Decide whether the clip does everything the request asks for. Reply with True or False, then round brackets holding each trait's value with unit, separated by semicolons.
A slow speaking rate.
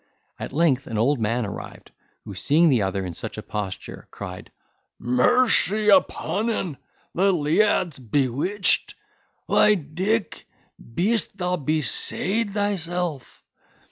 True (115 wpm)